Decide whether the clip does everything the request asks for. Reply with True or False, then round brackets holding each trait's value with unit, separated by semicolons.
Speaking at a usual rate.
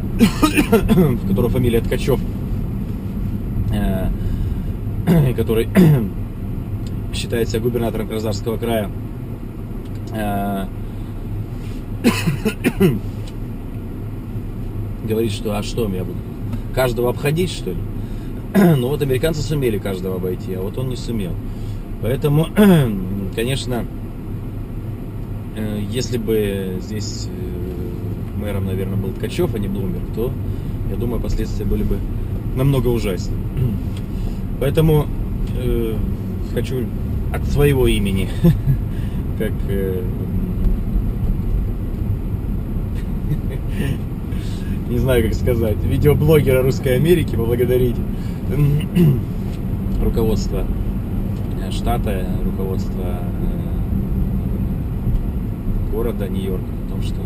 False (80 wpm)